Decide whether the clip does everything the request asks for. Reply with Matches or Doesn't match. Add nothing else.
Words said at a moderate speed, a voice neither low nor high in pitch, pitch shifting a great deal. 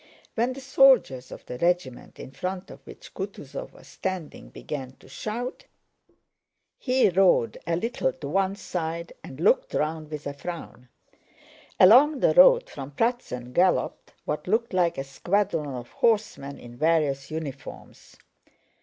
Matches